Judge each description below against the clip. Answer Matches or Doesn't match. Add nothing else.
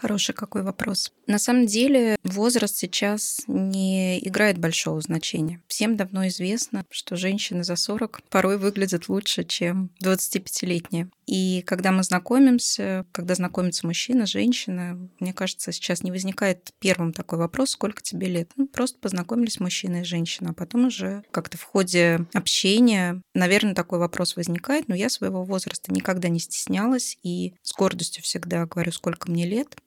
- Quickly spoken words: Doesn't match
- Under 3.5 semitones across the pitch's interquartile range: Matches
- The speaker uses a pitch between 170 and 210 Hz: Matches